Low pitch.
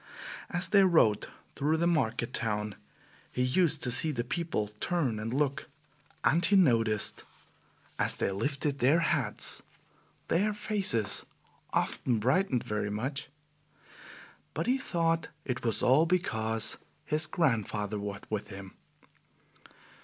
Yes: low, 130 Hz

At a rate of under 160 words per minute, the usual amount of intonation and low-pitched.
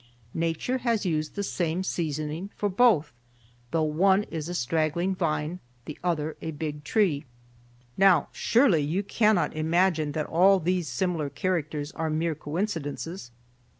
No: average, 140 wpm; average, 3.6 semitones; medium, 165 Hz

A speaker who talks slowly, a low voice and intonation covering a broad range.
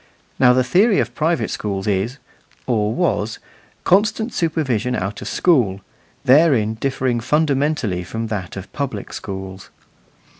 Yes: slow, 125 wpm; low, 125 Hz; wide, 6.7 semitones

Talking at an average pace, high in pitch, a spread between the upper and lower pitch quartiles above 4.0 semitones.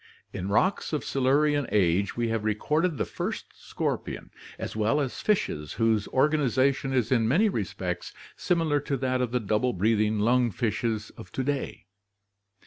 No: average, 155 wpm; low, 125 Hz; average, 4.9 semitones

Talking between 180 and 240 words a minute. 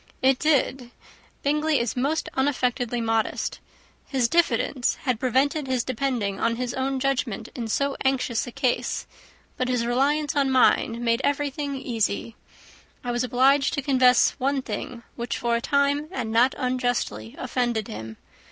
No: average, 150 wpm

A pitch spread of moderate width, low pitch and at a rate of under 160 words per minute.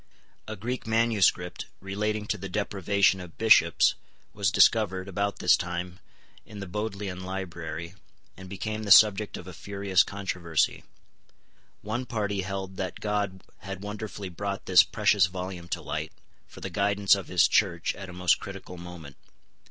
No: narrow, 2.3 semitones; very low, 95 Hz; average, 150 wpm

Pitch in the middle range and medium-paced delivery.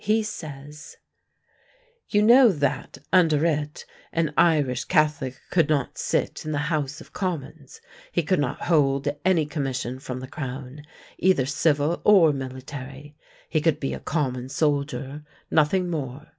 Yes: medium, 150 Hz; average, 145 wpm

